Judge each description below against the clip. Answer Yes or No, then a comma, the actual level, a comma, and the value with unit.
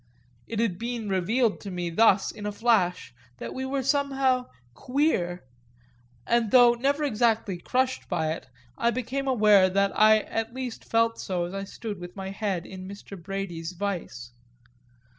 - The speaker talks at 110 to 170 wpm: Yes, average, 160 wpm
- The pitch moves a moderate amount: Yes, average, 4.6 semitones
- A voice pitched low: No, high, 210 Hz